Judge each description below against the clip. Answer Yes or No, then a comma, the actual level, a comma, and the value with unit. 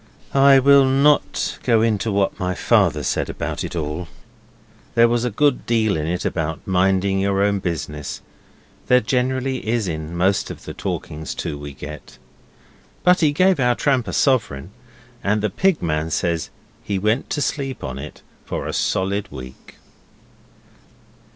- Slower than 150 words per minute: No, average, 160 wpm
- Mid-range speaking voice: No, low, 100 Hz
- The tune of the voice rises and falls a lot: Yes, wide, 7.4 semitones